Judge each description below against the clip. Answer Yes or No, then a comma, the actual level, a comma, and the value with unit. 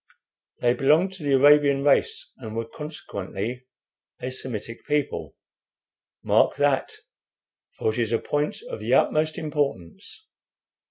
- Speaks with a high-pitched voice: No, medium, 140 Hz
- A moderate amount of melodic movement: Yes, average, 4.2 semitones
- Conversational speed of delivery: No, slow, 125 wpm